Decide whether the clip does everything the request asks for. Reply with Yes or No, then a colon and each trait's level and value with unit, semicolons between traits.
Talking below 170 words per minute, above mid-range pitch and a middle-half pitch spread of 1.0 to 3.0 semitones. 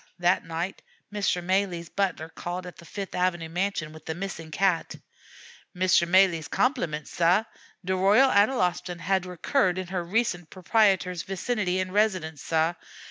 No: average, 145 wpm; medium, 180 Hz; narrow, 2.4 semitones